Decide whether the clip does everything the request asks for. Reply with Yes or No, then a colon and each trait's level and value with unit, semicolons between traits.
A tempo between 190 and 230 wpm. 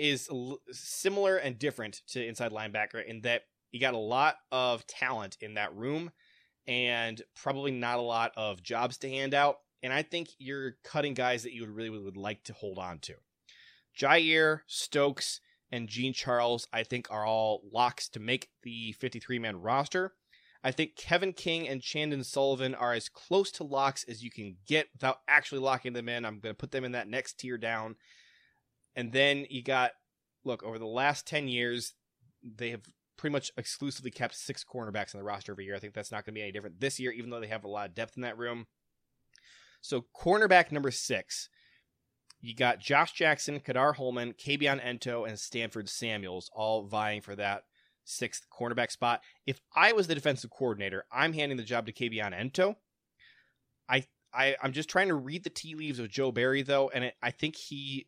Yes: average, 195 wpm